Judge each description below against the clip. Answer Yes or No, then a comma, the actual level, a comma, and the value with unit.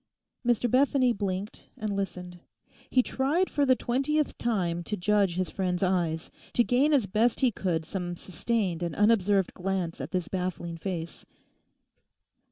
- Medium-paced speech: Yes, average, 150 wpm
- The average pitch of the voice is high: Yes, high, 195 Hz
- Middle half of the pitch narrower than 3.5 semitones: No, average, 5.2 semitones